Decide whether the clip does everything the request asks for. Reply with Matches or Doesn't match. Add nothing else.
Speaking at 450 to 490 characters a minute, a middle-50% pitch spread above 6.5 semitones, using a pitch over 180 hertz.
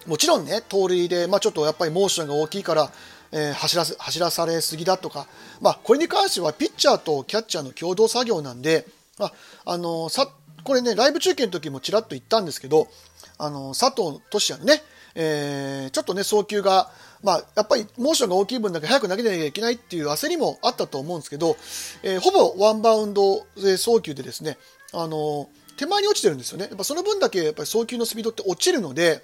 Matches